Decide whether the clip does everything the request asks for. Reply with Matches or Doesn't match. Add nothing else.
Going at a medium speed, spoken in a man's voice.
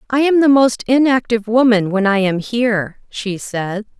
Doesn't match